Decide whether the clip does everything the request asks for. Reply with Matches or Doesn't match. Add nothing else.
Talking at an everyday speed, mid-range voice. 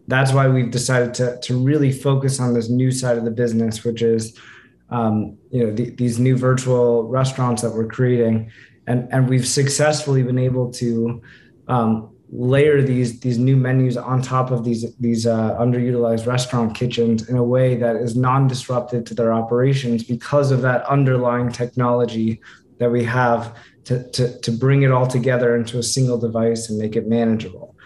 Doesn't match